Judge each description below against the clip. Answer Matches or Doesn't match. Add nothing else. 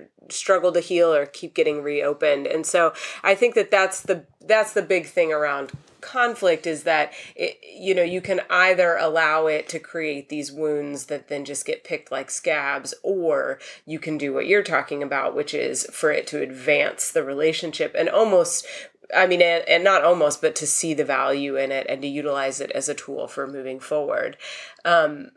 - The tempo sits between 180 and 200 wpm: Matches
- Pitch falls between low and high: Matches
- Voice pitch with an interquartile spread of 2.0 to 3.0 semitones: Doesn't match